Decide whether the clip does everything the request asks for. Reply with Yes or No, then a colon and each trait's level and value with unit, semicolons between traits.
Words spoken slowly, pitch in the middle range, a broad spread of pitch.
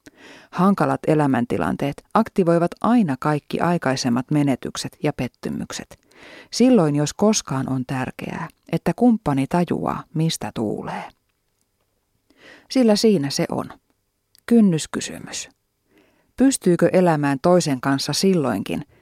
Yes: slow, 90 wpm; medium, 160 Hz; wide, 6.8 semitones